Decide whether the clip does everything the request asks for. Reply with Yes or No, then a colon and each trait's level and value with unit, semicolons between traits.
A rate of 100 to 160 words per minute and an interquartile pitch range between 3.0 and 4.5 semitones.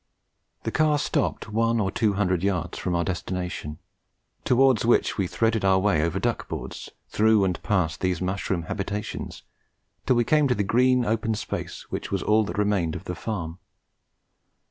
No: average, 170 wpm; average, 3.9 semitones